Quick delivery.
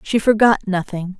No: average, 150 wpm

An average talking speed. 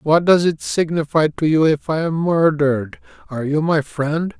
Yes: average, 190 wpm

